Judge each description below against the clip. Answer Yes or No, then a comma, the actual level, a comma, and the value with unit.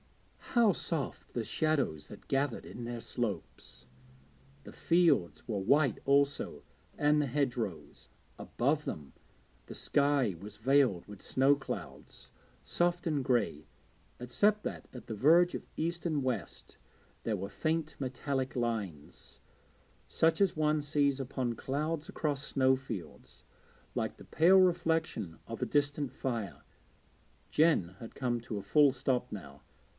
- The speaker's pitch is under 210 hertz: Yes, low, 135 Hz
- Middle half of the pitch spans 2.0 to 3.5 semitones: No, average, 4.9 semitones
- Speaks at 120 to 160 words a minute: Yes, slow, 135 wpm